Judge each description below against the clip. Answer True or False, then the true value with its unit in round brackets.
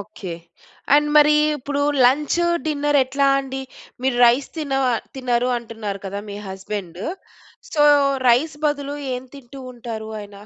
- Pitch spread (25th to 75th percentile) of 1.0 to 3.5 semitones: False (4.8 semitones)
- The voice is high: True (255 Hz)